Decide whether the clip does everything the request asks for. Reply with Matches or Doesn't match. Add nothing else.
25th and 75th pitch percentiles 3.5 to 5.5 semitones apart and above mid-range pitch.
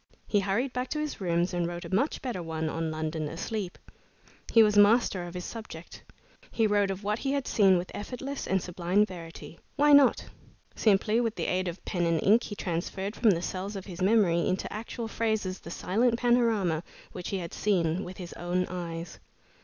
Matches